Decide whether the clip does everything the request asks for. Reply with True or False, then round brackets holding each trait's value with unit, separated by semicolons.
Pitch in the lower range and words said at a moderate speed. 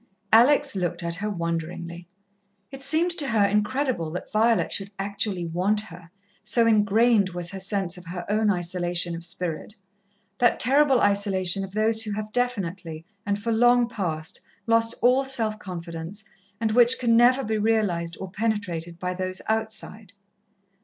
False (205 Hz; 155 wpm)